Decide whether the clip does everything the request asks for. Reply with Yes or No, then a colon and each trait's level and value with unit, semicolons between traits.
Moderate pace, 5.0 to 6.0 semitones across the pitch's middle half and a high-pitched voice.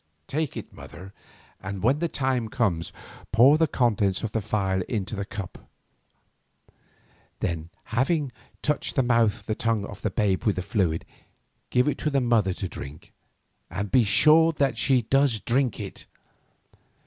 No: average, 165 wpm; average, 5.3 semitones; low, 115 Hz